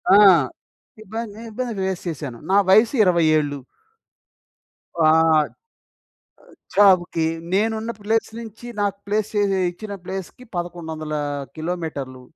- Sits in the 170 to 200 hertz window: Yes, high, 190 Hz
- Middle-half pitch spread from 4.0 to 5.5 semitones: Yes, average, 4.8 semitones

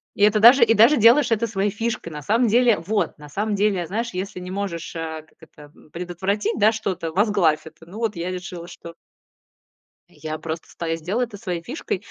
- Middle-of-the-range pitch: No, high, 195 Hz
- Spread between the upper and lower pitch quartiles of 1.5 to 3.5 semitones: No, average, 4.6 semitones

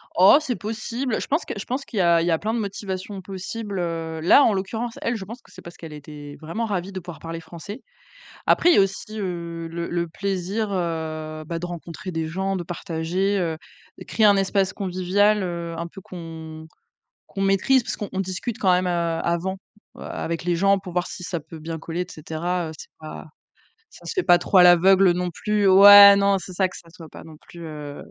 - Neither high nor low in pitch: Yes, medium, 180 Hz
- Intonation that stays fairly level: No, average, 3.1 semitones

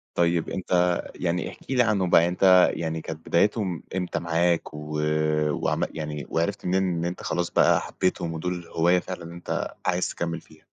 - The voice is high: No, very low, 85 Hz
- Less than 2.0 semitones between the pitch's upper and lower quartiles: Yes, narrow, 1.6 semitones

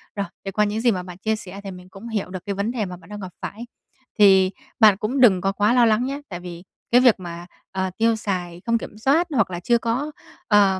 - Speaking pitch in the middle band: No, high, 205 Hz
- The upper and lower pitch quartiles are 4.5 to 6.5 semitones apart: No, average, 3.6 semitones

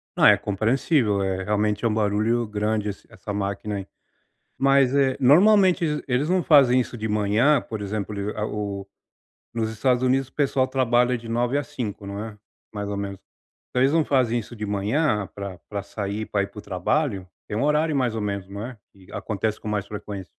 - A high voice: No, low, 110 Hz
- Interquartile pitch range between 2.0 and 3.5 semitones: No, average, 4.2 semitones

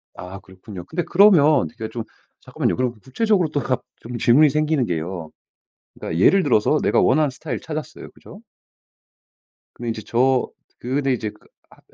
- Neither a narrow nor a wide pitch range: No, wide, 5.8 semitones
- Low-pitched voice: Yes, low, 130 Hz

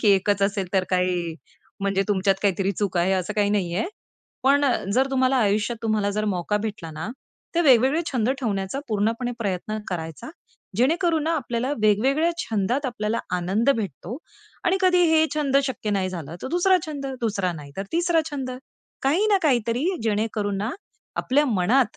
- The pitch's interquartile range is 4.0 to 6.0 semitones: Yes, wide, 5.4 semitones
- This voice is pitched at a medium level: No, high, 215 Hz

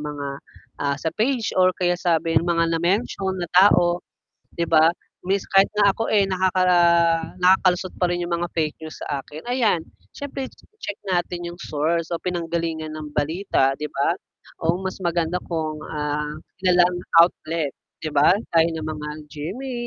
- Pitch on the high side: No, medium, 170 Hz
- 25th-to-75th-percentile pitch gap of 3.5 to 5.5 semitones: No, average, 2.9 semitones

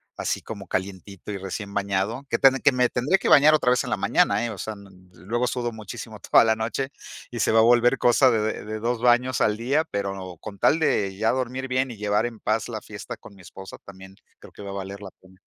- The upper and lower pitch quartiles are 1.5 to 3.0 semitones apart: No, average, 3.7 semitones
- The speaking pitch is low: Yes, low, 110 Hz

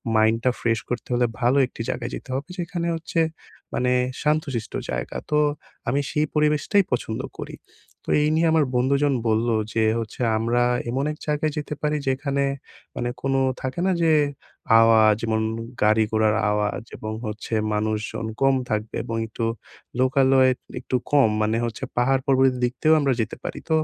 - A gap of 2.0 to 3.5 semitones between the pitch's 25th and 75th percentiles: No, average, 4.5 semitones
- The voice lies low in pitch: Yes, low, 125 Hz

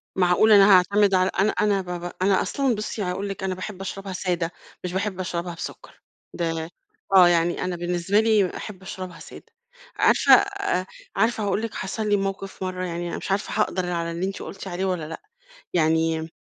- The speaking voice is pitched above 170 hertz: Yes, medium, 185 Hz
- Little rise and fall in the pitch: Yes, narrow, 2.3 semitones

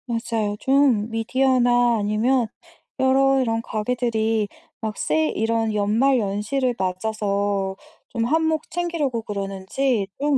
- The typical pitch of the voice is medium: No, high, 230 Hz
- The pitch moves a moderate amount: Yes, average, 4.0 semitones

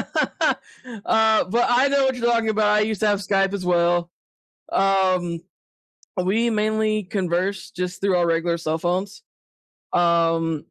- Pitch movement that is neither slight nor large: Yes, average, 3.7 semitones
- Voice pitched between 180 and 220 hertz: Yes, high, 190 Hz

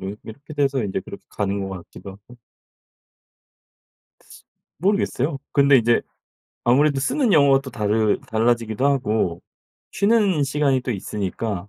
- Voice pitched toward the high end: No, low, 125 Hz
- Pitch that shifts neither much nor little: Yes, average, 5.0 semitones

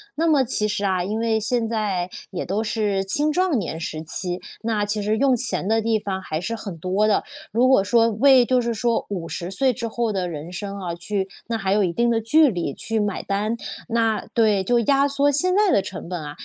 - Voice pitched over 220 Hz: No, high, 215 Hz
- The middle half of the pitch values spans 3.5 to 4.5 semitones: Yes, average, 3.8 semitones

